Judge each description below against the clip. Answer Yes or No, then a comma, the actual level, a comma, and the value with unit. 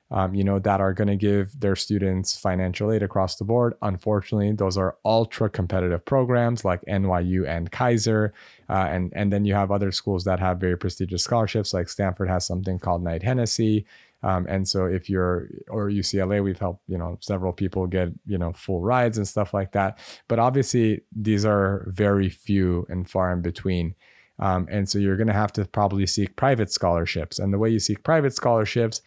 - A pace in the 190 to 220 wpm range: Yes, average, 200 wpm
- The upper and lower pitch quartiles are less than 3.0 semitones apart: Yes, narrow, 2.4 semitones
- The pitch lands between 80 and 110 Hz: Yes, low, 100 Hz